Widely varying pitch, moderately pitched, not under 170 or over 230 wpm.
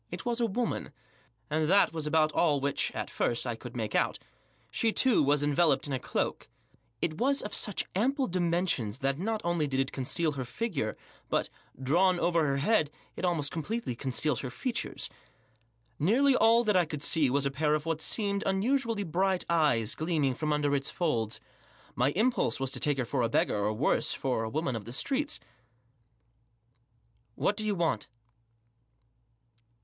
Yes: wide, 6.6 semitones; medium, 155 Hz; average, 180 wpm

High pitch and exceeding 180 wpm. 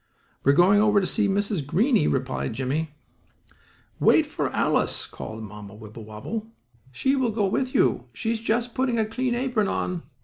No: high, 205 Hz; average, 170 wpm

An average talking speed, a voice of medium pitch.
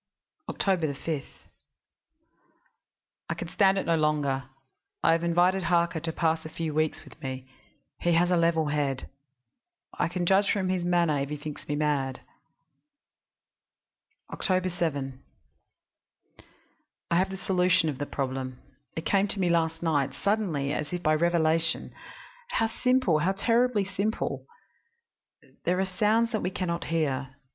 Yes: average, 145 wpm; medium, 170 Hz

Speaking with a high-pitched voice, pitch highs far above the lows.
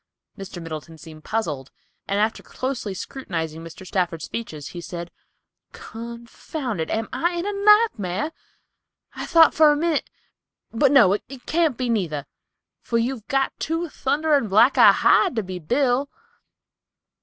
Yes: high, 230 Hz; wide, 8.3 semitones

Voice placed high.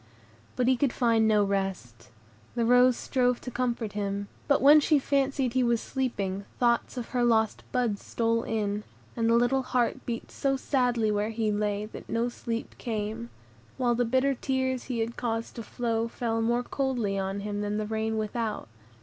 Yes: high, 230 Hz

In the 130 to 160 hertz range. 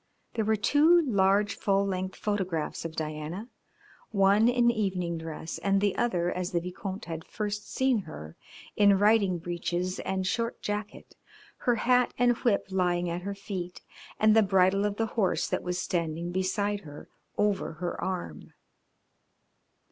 No: high, 195 Hz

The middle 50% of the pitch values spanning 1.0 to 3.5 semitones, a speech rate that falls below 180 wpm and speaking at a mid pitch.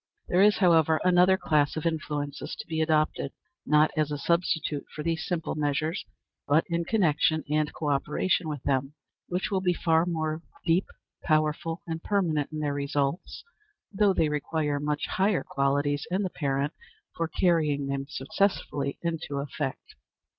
Yes: average, 2.7 semitones; average, 155 wpm; medium, 155 Hz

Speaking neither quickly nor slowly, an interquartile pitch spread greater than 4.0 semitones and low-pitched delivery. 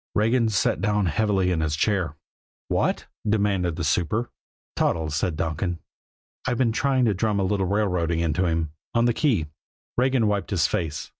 Yes: average, 165 wpm; average, 4.7 semitones; very low, 95 Hz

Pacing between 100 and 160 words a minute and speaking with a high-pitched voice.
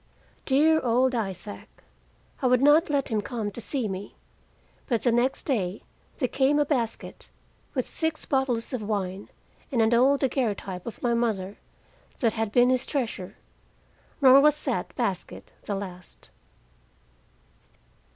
Yes: average, 140 wpm; high, 240 Hz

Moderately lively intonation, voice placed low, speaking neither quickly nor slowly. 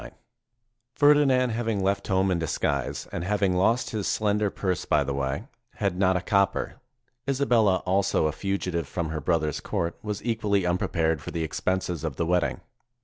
Yes: average, 3.9 semitones; very low, 95 Hz; average, 170 wpm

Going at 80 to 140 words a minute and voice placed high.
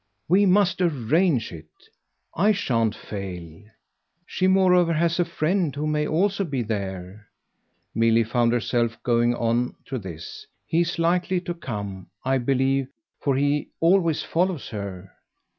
No: slow, 135 wpm; low, 135 Hz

